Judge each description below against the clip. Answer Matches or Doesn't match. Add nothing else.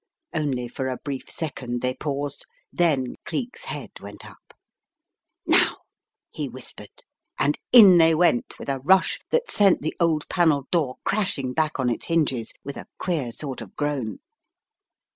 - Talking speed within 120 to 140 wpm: Doesn't match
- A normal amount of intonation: Matches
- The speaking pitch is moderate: Matches